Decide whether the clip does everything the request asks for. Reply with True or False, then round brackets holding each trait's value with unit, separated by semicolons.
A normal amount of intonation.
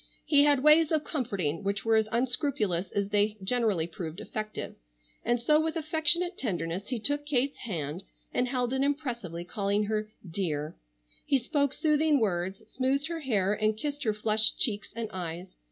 False (6.3 semitones)